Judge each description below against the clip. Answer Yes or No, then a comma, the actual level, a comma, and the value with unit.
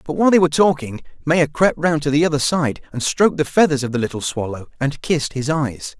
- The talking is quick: Yes, fast, 240 wpm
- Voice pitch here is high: No, medium, 145 Hz